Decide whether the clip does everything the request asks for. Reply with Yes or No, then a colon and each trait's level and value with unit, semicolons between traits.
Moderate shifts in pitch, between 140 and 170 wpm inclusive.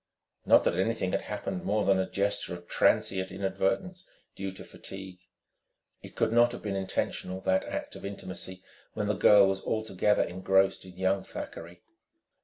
No: narrow, 1.6 semitones; average, 165 wpm